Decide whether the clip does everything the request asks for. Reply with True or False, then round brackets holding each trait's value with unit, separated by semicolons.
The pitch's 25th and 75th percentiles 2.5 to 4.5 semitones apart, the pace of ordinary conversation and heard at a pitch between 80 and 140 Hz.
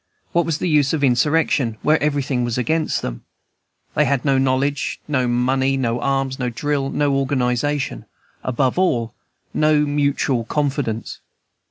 True (2.9 semitones; 145 wpm; 135 Hz)